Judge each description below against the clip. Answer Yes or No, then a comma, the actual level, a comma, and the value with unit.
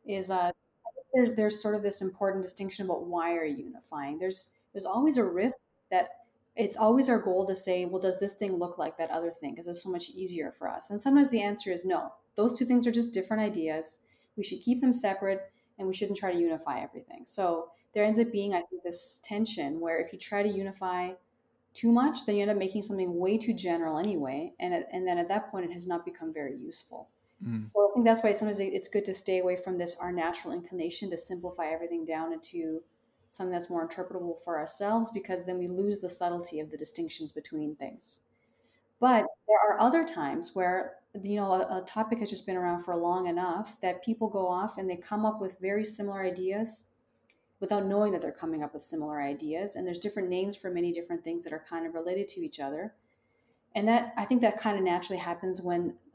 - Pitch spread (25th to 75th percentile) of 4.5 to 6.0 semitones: No, average, 3.6 semitones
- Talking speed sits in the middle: No, fast, 225 wpm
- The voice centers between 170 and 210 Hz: Yes, high, 190 Hz